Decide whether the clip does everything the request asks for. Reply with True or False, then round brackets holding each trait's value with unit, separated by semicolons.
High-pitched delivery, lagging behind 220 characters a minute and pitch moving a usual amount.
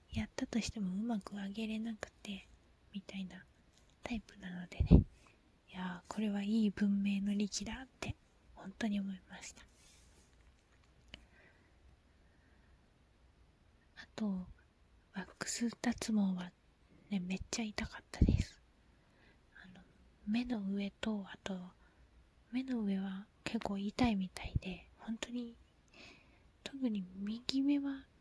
True (200 Hz; 210 characters per minute; 3.7 semitones)